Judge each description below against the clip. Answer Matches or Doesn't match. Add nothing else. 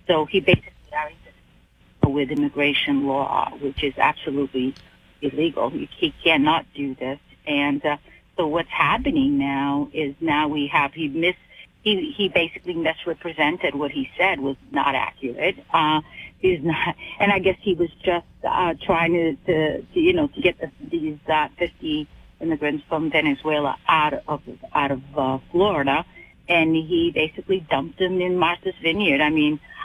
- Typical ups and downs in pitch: Matches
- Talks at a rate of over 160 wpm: Doesn't match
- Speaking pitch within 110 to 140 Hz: Doesn't match